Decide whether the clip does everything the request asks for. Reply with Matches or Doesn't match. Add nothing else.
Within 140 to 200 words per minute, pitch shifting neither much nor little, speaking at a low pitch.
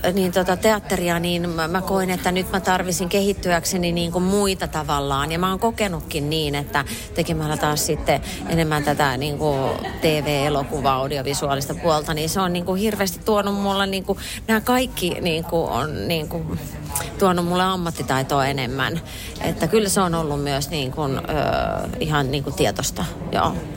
Doesn't match